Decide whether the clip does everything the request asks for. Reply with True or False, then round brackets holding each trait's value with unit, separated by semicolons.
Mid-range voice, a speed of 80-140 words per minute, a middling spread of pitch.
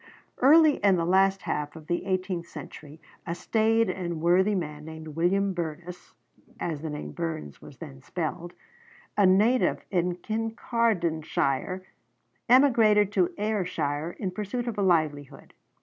True (180 Hz; 135 wpm; 4.4 semitones)